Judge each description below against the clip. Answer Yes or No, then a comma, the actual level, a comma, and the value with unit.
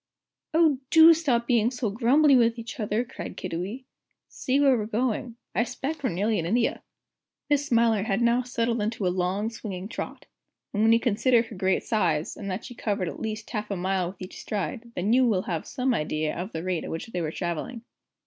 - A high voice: Yes, high, 225 Hz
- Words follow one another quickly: Yes, fast, 210 wpm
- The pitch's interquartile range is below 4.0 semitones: No, average, 4.5 semitones